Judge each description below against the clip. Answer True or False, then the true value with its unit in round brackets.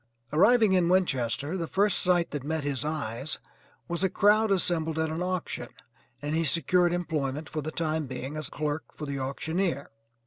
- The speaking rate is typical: True (175 wpm)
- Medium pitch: True (160 Hz)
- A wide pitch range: False (3.5 semitones)